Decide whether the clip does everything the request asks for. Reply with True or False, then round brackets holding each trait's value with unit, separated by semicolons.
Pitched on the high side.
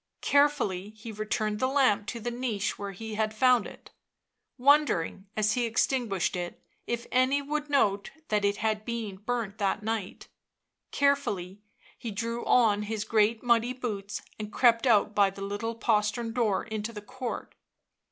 True (220 Hz)